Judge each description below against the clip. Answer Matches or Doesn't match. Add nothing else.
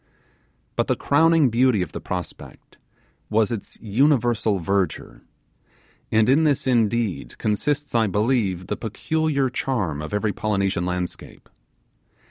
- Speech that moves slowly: Matches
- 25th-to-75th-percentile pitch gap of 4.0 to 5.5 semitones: Matches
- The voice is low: Matches